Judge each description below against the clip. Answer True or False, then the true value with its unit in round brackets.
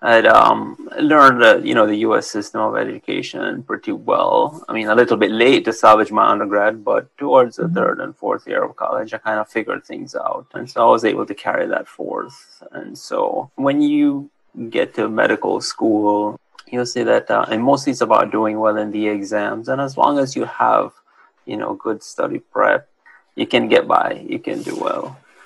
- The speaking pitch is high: False (140 Hz)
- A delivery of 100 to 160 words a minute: False (205 wpm)